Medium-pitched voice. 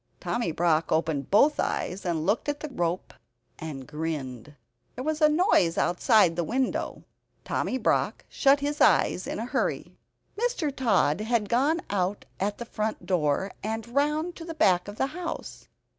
No: high, 215 Hz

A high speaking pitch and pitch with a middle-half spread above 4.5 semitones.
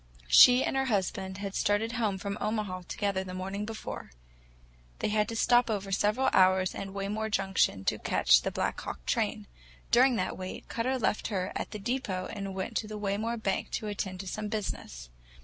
No: high, 205 Hz; narrow, 2.6 semitones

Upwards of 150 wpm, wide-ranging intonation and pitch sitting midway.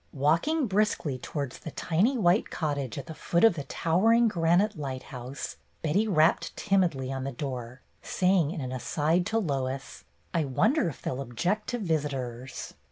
Yes: average, 165 wpm; wide, 6.4 semitones; medium, 155 Hz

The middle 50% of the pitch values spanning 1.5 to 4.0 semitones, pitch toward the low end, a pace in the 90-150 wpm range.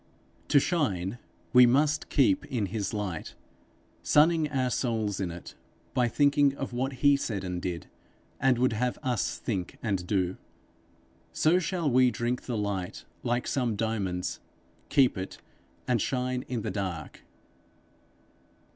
No: average, 5.3 semitones; low, 120 Hz; average, 140 wpm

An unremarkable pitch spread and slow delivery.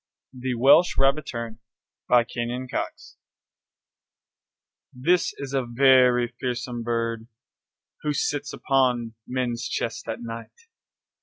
No: narrow, 2.3 semitones; slow, 100 wpm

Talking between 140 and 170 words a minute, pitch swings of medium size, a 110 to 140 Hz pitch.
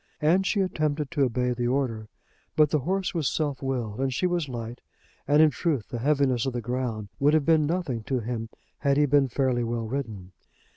No: fast, 205 wpm; average, 3.9 semitones; low, 135 Hz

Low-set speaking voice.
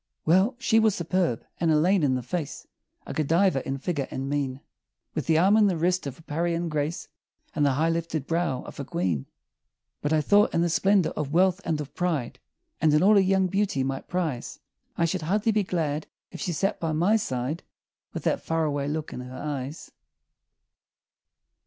No: medium, 160 Hz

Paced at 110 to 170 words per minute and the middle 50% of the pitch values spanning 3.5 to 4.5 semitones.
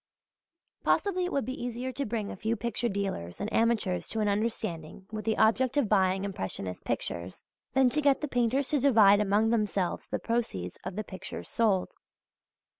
No: average, 180 wpm; average, 4.0 semitones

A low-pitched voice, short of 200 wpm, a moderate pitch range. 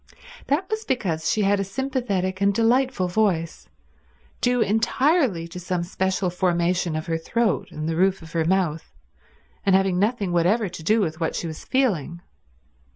No: high, 190 Hz; average, 165 wpm; average, 4.8 semitones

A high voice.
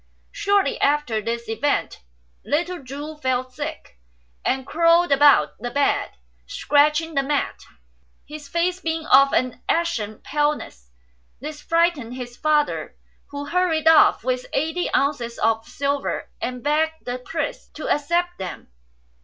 Yes: very high, 290 Hz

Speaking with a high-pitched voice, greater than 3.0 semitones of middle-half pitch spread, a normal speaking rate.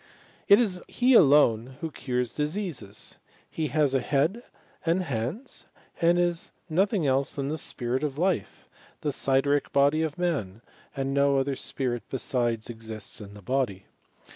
No: medium, 140 Hz; average, 4.8 semitones; average, 150 wpm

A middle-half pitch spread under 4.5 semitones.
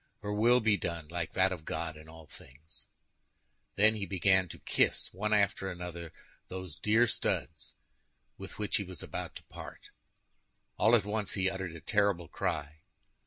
Yes: average, 3.8 semitones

